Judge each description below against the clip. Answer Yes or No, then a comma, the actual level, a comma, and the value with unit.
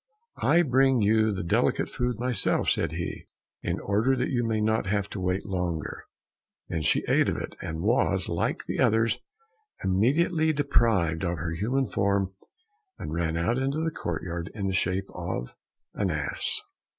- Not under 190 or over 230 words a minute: No, average, 165 wpm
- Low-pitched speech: Yes, low, 100 Hz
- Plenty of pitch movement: Yes, wide, 6.0 semitones